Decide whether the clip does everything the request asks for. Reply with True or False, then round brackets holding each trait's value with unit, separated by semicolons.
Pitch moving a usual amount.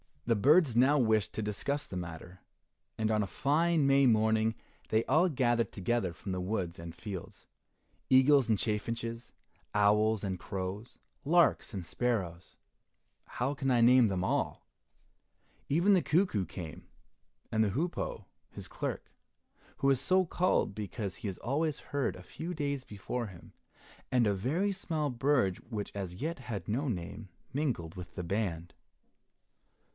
False (6.2 semitones)